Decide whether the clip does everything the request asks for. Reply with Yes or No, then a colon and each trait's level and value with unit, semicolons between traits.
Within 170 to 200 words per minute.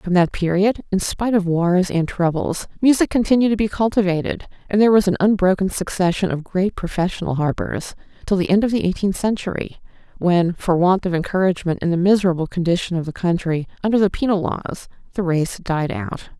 Yes: average, 185 wpm